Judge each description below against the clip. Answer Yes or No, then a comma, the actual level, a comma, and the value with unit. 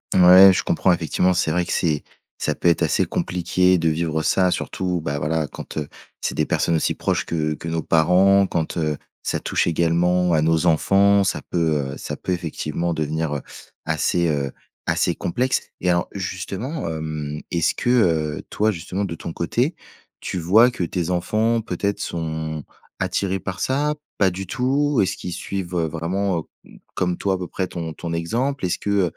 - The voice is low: Yes, very low, 90 Hz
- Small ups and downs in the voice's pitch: No, average, 3.0 semitones